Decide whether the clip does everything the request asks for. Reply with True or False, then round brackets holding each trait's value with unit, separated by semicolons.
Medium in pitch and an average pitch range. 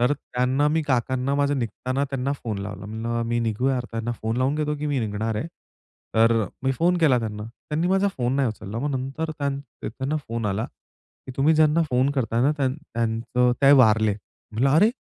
False (130 Hz; 3.9 semitones)